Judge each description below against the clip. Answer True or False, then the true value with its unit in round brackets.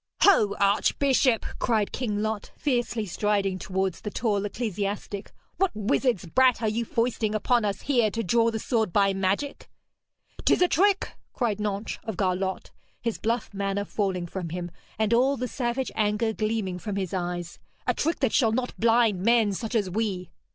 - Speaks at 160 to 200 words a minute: True (170 wpm)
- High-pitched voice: True (215 Hz)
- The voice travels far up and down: False (3.2 semitones)